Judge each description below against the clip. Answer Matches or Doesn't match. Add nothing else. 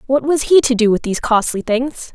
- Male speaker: Doesn't match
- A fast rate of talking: Matches